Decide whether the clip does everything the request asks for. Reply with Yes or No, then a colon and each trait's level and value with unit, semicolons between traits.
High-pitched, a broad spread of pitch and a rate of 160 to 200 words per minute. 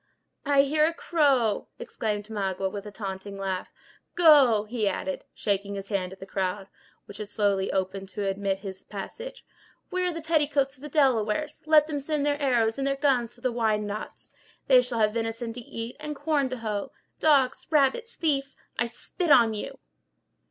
Yes: high, 230 Hz; wide, 6.0 semitones; average, 180 wpm